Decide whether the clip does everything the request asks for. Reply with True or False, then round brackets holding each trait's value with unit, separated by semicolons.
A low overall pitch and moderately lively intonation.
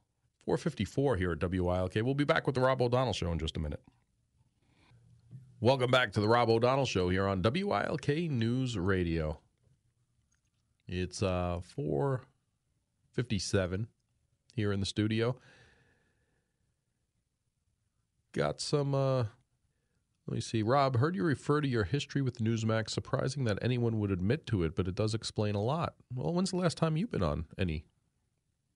True (115 Hz; 4.8 semitones)